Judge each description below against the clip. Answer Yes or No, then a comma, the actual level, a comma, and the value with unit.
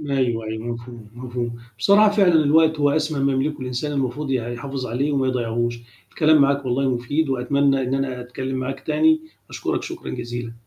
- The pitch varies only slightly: No, average, 3.1 semitones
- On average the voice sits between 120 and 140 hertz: Yes, low, 135 Hz